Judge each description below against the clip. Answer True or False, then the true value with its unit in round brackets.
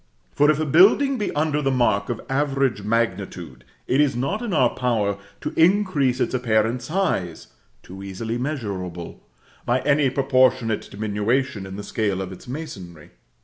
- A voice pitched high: False (125 Hz)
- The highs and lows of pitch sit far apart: True (6.1 semitones)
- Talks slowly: False (155 wpm)